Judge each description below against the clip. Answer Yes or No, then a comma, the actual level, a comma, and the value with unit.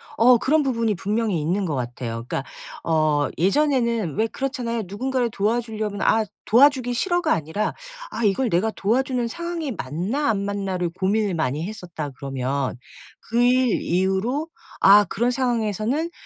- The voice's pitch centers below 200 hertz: No, high, 215 Hz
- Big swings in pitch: Yes, wide, 5.7 semitones